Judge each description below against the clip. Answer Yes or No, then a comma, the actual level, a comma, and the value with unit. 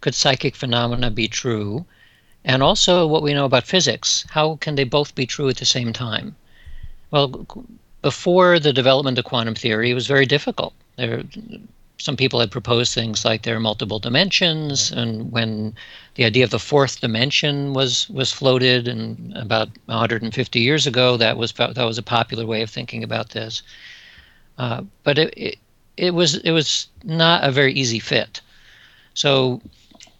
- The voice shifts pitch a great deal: No, average, 4.0 semitones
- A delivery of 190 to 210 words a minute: No, average, 170 wpm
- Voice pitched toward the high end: No, low, 125 Hz